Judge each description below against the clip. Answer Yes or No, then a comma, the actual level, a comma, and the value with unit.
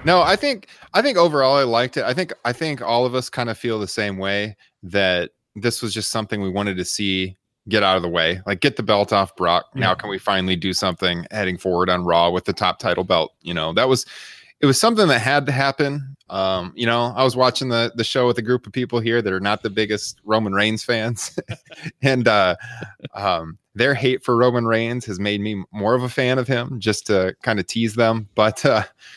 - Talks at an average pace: No, fast, 240 wpm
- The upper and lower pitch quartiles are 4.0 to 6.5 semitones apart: Yes, average, 4.3 semitones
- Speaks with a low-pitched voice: Yes, low, 115 Hz